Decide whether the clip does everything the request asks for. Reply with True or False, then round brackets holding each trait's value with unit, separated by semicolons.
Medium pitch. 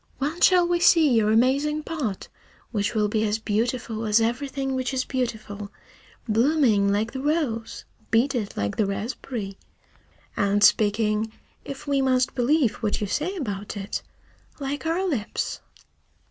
False (235 Hz)